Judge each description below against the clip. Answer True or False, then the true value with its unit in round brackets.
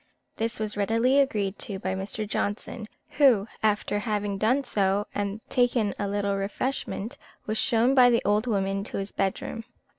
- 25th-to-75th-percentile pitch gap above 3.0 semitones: False (2.6 semitones)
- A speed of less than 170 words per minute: True (160 wpm)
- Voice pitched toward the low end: False (210 Hz)